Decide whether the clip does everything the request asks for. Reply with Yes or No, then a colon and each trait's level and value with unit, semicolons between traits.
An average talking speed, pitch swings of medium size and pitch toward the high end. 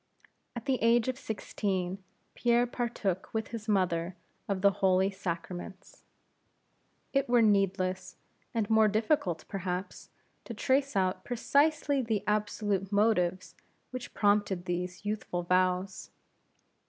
No: slow, 115 wpm; average, 3.7 semitones; high, 200 Hz